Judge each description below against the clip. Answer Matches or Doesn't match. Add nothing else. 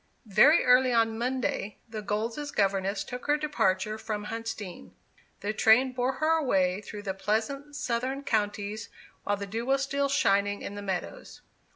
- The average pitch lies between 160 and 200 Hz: Doesn't match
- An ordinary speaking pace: Matches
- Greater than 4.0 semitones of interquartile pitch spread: Matches